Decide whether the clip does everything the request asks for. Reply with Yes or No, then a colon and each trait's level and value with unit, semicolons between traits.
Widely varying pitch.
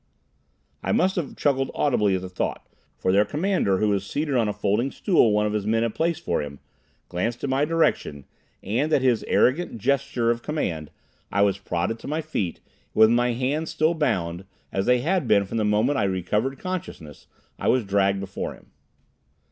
Yes: wide, 6.6 semitones